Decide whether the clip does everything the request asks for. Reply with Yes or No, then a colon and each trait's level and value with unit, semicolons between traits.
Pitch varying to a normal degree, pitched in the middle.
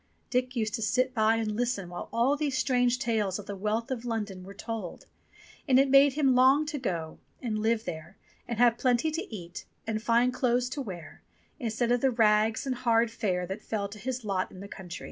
No: average, 3.4 semitones; high, 230 Hz